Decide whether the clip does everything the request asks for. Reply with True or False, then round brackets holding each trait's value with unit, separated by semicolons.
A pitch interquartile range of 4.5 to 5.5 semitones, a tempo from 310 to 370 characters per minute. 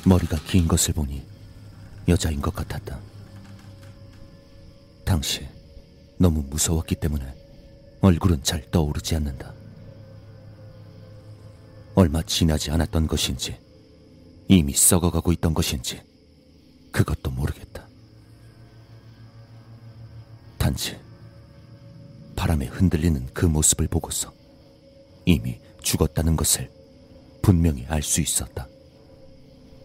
False (5.1 semitones; 195 characters per minute)